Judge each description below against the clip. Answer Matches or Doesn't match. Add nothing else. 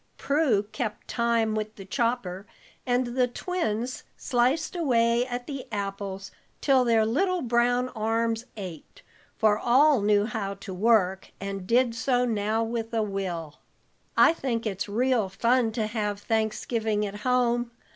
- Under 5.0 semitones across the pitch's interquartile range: Matches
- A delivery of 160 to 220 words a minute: Doesn't match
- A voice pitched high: Matches